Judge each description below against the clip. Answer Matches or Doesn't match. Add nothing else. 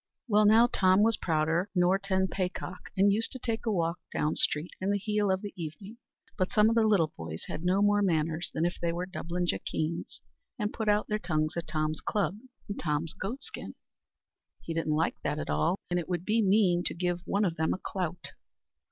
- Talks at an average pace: Doesn't match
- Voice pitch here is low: Doesn't match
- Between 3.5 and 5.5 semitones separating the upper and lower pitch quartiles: Matches